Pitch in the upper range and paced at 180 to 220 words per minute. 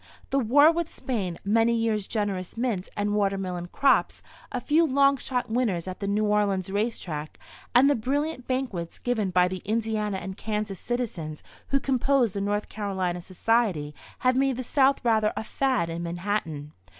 No: high, 215 Hz; average, 170 wpm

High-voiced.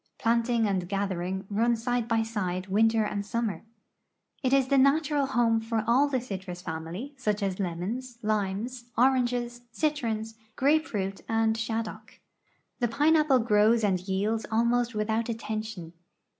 Yes: high, 225 Hz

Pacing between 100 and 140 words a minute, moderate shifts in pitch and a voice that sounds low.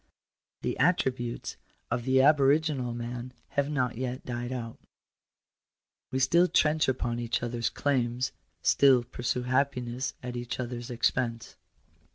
No: slow, 135 wpm; narrow, 1.9 semitones; low, 125 Hz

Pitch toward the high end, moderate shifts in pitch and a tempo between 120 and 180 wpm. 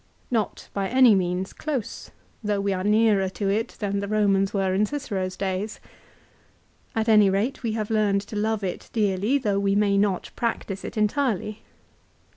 No: high, 205 Hz; narrow, 2.0 semitones; average, 170 wpm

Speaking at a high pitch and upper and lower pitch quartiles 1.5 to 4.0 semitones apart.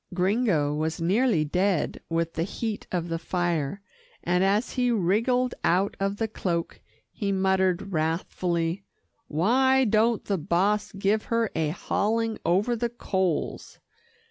No: high, 195 Hz; average, 4.5 semitones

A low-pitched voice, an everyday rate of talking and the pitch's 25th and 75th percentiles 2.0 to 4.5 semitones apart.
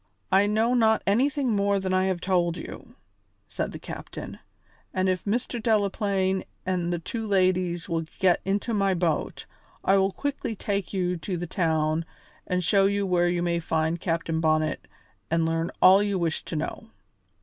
No: medium, 185 Hz; average, 170 wpm; average, 2.9 semitones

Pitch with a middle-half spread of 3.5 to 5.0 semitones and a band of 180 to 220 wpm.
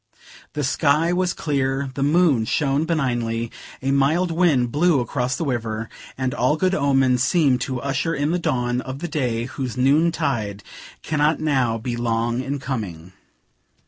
No: average, 3.8 semitones; average, 155 wpm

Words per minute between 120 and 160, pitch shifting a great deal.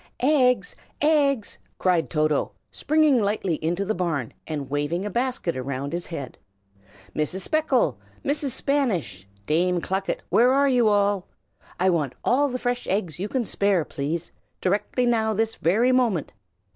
Yes: average, 145 wpm; wide, 7.0 semitones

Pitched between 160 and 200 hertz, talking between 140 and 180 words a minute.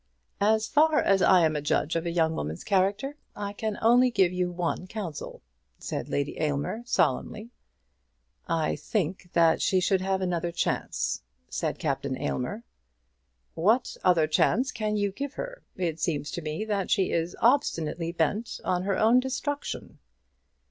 Yes: medium, 185 Hz; average, 155 wpm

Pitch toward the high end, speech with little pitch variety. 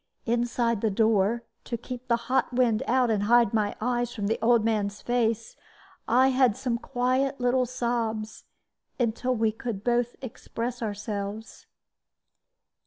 Yes: high, 235 Hz; narrow, 2.1 semitones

